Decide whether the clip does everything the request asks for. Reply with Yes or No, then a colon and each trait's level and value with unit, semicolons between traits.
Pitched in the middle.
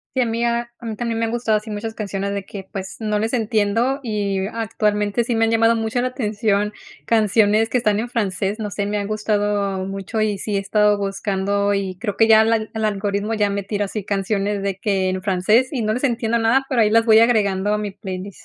No: high, 210 Hz